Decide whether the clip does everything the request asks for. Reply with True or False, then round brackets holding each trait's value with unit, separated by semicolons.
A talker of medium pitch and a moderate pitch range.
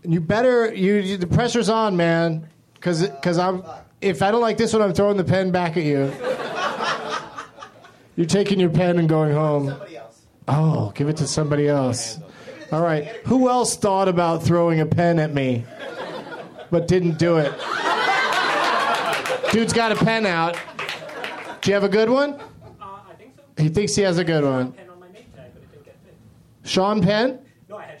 True (175 Hz; 4.6 semitones)